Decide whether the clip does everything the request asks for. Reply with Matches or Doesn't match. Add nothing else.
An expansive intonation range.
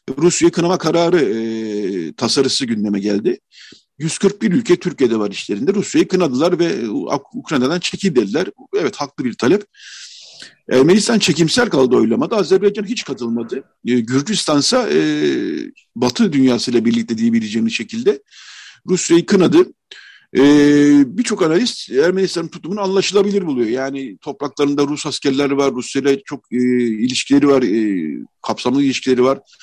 Matches